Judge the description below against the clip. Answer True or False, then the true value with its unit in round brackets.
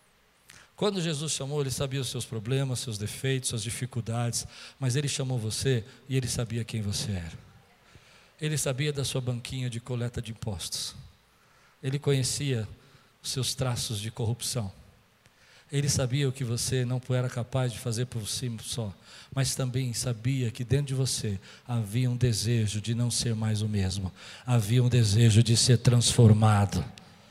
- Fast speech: False (160 wpm)